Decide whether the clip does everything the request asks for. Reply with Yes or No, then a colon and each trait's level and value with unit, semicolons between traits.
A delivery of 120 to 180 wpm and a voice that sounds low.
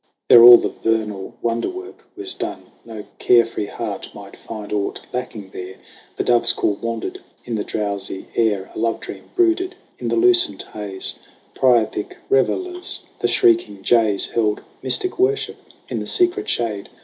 Yes: average, 160 wpm; low, 115 Hz